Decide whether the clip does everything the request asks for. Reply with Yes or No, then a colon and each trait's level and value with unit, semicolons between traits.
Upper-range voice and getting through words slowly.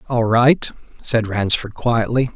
No: low, 115 Hz; slow, 125 wpm